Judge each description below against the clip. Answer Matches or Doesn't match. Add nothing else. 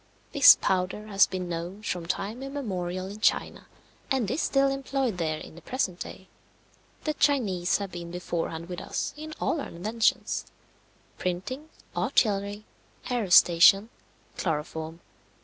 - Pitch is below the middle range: Doesn't match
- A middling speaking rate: Doesn't match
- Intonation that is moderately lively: Doesn't match